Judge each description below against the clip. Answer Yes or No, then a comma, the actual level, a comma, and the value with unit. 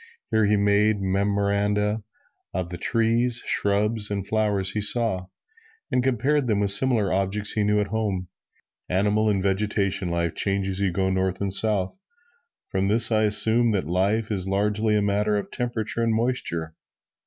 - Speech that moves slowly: No, average, 165 wpm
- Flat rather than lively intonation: Yes, narrow, 2.1 semitones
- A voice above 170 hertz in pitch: No, low, 105 Hz